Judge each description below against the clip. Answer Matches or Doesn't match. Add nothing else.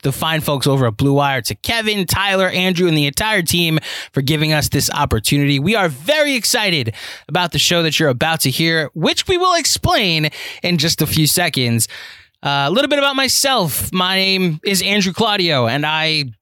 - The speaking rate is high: Doesn't match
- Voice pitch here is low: Doesn't match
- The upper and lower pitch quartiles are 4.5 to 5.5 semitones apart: Matches